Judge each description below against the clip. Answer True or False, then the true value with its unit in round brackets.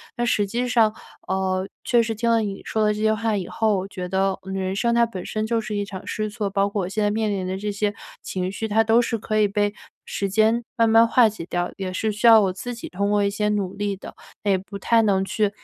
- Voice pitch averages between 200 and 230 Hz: True (210 Hz)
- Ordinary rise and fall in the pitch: False (2.3 semitones)